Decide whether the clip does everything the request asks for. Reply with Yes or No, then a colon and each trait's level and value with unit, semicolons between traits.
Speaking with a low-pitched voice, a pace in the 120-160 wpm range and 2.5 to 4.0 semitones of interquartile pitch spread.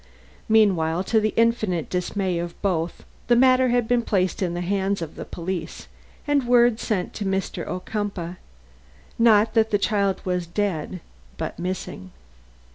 No: high, 195 Hz; average, 150 wpm; average, 3.7 semitones